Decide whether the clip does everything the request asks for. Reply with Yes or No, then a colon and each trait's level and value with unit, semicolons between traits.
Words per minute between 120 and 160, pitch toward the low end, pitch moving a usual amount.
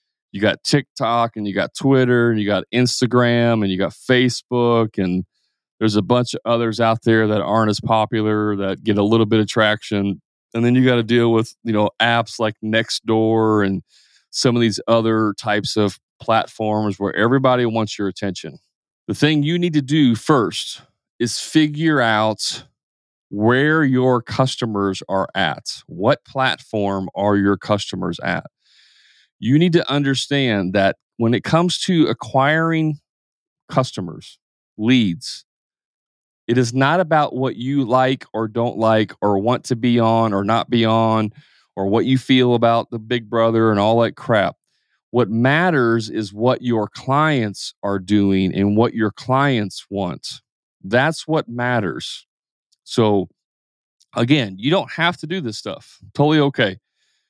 Yes: average, 155 wpm; low, 115 Hz; average, 3.6 semitones